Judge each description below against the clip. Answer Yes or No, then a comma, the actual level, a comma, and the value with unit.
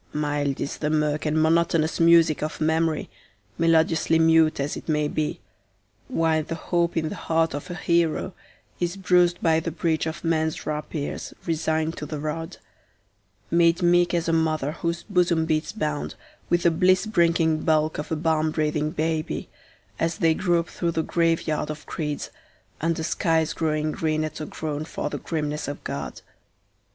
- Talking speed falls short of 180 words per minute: Yes, average, 165 wpm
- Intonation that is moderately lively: No, narrow, 1.5 semitones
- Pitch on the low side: No, medium, 160 Hz